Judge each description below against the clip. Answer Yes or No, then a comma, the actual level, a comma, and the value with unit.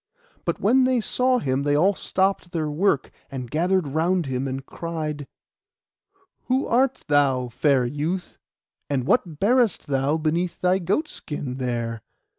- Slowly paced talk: No, average, 145 wpm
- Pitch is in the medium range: Yes, medium, 155 Hz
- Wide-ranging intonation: Yes, wide, 5.8 semitones